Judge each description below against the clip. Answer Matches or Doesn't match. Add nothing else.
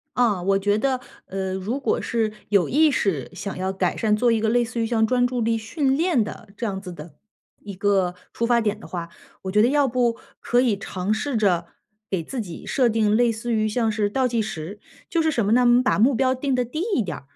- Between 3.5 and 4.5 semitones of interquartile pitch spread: Matches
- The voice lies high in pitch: Matches